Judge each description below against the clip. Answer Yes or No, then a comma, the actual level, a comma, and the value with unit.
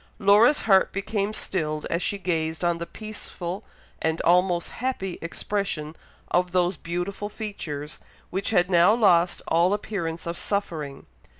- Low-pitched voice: No, medium, 180 Hz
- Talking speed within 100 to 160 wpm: Yes, slow, 135 wpm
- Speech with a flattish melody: No, average, 3.2 semitones